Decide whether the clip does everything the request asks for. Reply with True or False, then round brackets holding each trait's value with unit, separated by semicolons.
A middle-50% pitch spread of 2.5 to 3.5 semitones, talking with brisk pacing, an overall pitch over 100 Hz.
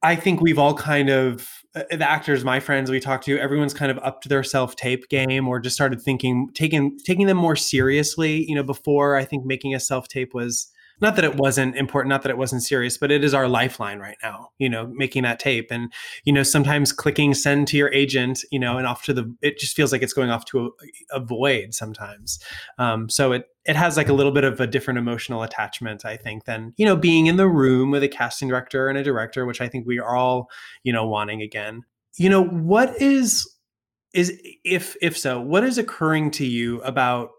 True (2.8 semitones; 230 wpm; 135 Hz)